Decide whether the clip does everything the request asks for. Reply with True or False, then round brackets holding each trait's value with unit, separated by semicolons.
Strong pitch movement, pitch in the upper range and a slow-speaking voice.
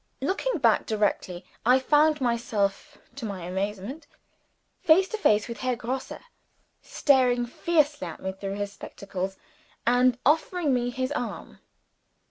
True (6.0 semitones; 245 Hz; 130 wpm)